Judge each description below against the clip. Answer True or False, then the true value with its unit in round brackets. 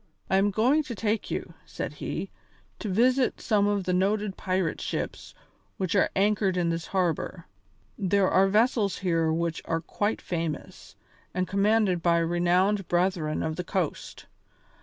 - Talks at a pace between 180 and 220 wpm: False (155 wpm)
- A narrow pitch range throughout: False (3.1 semitones)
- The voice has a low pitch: False (190 Hz)